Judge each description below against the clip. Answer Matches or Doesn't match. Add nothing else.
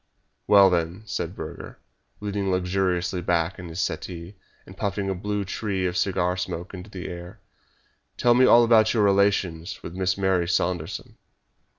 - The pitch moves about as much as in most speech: Doesn't match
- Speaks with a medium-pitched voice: Doesn't match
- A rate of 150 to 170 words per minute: Matches